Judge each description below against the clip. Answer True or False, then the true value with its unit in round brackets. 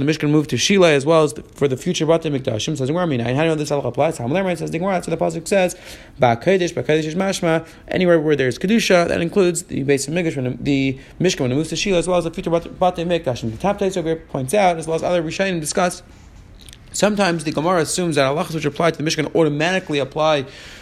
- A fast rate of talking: True (210 wpm)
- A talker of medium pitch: True (160 Hz)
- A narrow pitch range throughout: False (4.0 semitones)